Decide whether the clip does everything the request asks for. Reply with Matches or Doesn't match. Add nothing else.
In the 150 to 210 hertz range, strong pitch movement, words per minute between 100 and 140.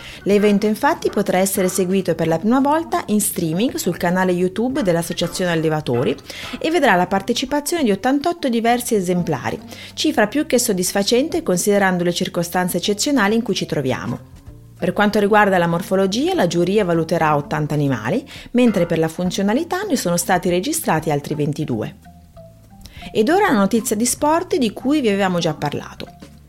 Doesn't match